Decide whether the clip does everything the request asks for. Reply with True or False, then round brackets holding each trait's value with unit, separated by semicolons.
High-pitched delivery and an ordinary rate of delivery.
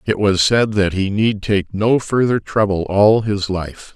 False (100 Hz; 195 wpm)